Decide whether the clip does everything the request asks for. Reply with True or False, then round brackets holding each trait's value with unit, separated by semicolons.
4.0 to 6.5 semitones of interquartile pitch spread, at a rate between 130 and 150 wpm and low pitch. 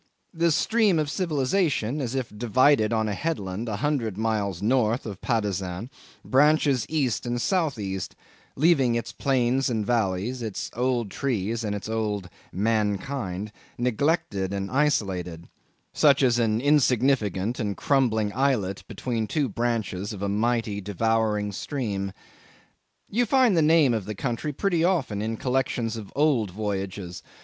True (5.0 semitones; 145 wpm; 115 Hz)